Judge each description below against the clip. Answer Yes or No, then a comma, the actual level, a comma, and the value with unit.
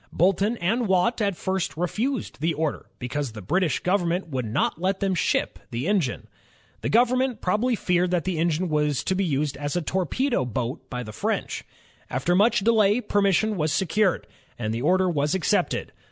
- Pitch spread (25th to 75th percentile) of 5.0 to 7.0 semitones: Yes, wide, 5.4 semitones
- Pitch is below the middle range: No, medium, 180 Hz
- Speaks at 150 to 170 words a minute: No, average, 180 wpm